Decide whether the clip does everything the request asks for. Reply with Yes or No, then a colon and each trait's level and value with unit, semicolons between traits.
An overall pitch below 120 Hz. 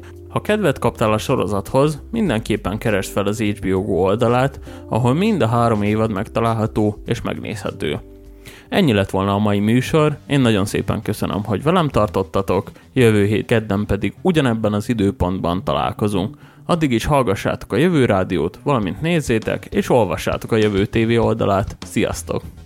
Yes: low, 110 Hz